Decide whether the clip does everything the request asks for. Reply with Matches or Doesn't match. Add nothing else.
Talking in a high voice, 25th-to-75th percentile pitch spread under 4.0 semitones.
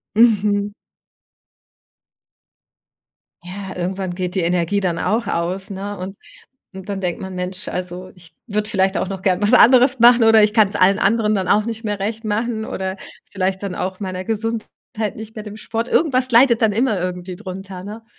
Matches